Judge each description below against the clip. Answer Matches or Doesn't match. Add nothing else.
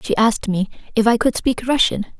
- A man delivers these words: Doesn't match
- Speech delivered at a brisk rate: Matches